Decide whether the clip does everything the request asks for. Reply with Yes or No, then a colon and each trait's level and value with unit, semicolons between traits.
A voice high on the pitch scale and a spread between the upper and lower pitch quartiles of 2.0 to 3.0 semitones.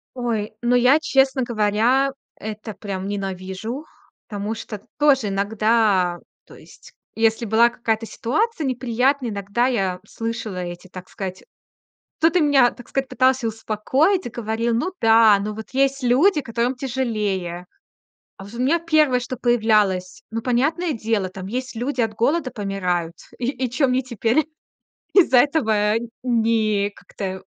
No: high, 230 Hz; average, 4.0 semitones